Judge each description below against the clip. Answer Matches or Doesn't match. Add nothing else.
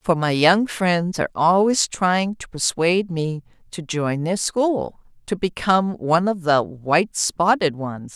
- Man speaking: Doesn't match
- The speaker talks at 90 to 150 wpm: Doesn't match